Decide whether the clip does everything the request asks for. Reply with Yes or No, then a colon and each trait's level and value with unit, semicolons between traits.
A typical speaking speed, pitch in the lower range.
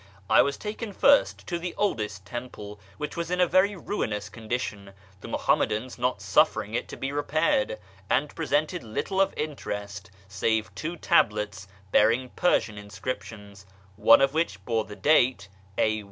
Yes: average, 155 wpm; low, 125 Hz